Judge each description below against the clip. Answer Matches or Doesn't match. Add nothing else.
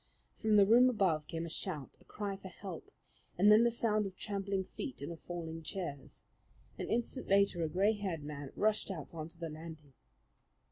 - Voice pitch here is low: Doesn't match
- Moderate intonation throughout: Matches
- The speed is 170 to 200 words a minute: Matches